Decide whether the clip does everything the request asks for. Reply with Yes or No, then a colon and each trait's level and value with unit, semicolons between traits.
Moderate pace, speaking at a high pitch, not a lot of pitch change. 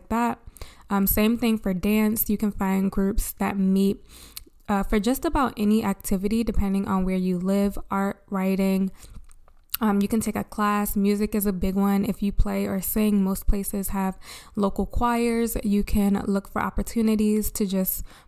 Yes: average, 175 wpm; high, 200 Hz; narrow, 1.6 semitones